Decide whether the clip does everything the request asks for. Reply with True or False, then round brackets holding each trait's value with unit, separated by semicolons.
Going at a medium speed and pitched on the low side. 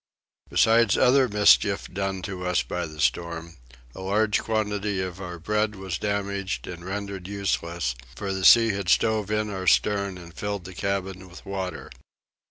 True (165 wpm; 95 Hz)